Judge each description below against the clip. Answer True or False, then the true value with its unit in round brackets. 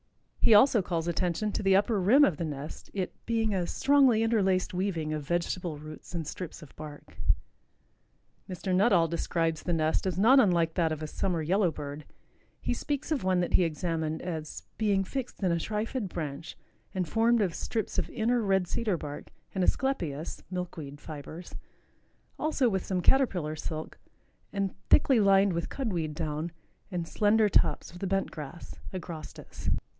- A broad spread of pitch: False (4.6 semitones)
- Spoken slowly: False (170 wpm)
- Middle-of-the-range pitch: True (180 Hz)